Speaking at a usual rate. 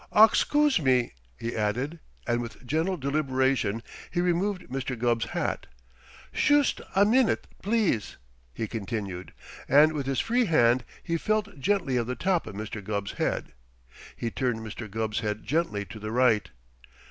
Yes: average, 150 wpm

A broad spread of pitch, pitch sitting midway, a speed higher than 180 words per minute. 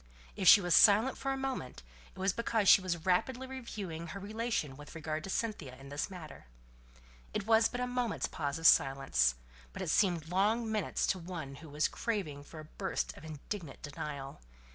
Yes: wide, 6.5 semitones; medium, 180 Hz; average, 190 wpm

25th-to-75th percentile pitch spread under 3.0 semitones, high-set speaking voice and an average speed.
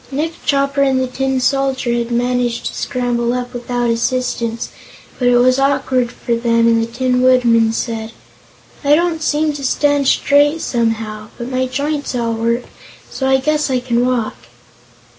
Yes: narrow, 2.5 semitones; very high, 250 Hz; average, 165 wpm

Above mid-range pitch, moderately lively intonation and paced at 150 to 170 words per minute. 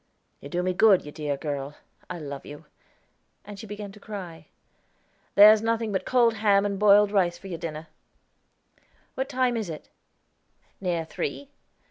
Yes: high, 195 Hz; average, 4.6 semitones; average, 160 wpm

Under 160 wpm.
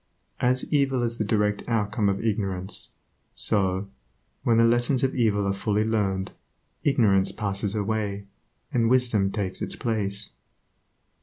Yes: slow, 135 wpm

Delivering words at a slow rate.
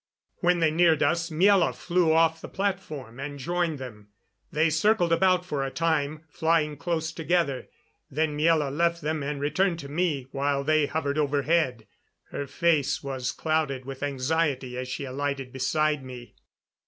No: average, 155 wpm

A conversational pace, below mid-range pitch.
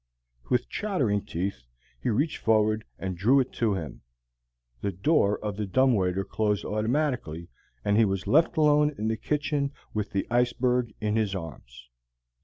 Yes: average, 160 wpm; low, 110 Hz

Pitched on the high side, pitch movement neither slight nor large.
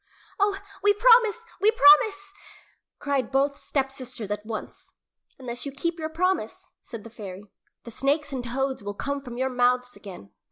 Yes: very high, 270 Hz; average, 5.0 semitones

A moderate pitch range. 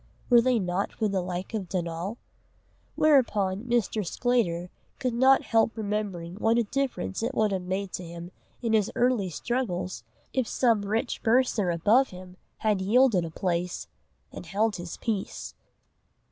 Yes: average, 4.6 semitones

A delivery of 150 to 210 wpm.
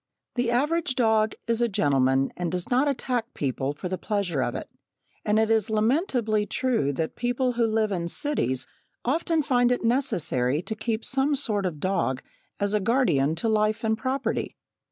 Yes: average, 180 wpm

